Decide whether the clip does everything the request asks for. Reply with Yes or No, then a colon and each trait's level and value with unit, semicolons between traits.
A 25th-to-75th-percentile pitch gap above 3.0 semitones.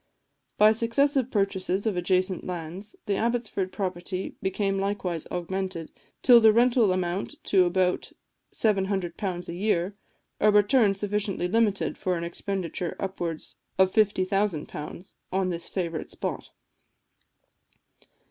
No: average, 2.7 semitones